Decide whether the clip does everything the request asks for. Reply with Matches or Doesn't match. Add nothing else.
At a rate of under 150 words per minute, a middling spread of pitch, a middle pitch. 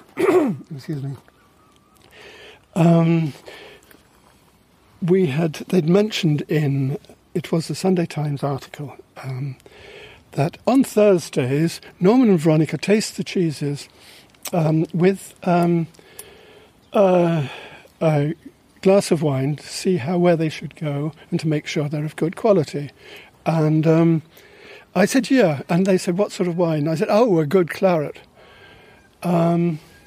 Matches